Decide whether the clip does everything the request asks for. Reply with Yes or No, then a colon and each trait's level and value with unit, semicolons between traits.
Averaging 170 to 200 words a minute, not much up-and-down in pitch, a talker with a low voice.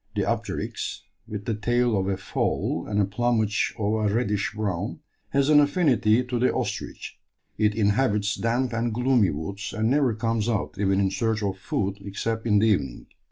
No: average, 180 wpm; average, 3.0 semitones; low, 110 Hz